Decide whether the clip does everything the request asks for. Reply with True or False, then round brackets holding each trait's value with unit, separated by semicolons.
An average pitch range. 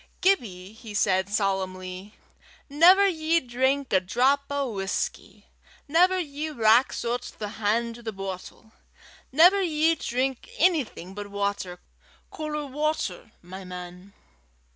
False (7.5 semitones)